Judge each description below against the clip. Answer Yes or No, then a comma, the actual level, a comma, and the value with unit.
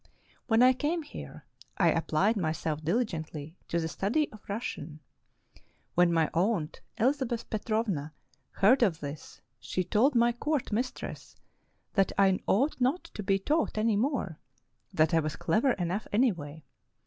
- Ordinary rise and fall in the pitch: No, wide, 6.8 semitones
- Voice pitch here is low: No, high, 205 Hz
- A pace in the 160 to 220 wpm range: No, average, 150 wpm